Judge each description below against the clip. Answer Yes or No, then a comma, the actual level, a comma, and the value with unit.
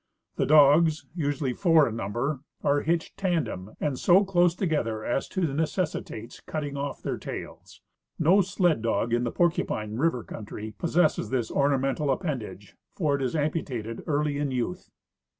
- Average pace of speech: Yes, average, 155 wpm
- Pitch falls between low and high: Yes, medium, 145 Hz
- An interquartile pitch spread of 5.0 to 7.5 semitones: Yes, wide, 5.5 semitones